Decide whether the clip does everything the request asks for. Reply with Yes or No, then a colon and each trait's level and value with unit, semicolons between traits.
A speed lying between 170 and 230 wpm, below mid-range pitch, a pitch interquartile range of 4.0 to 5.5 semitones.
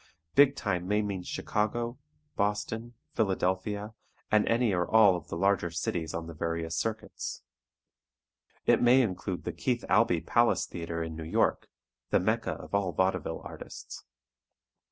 No: average, 140 wpm; low, 100 Hz; average, 4.4 semitones